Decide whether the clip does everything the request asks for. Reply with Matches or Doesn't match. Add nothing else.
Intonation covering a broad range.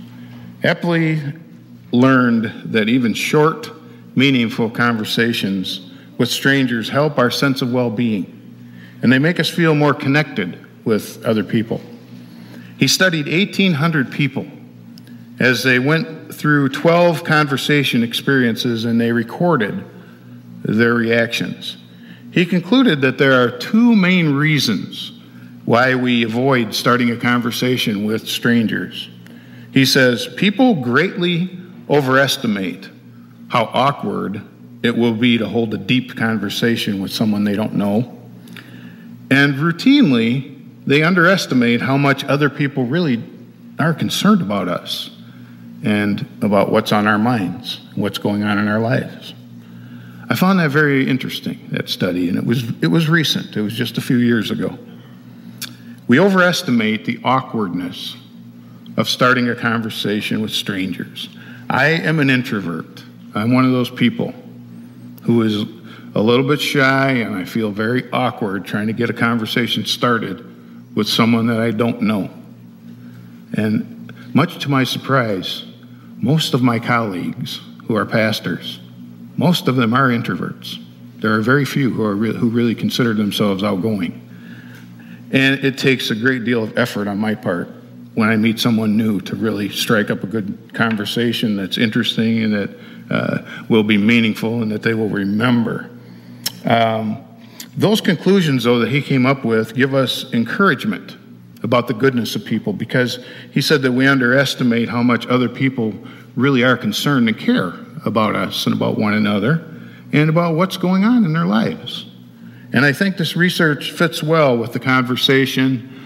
Matches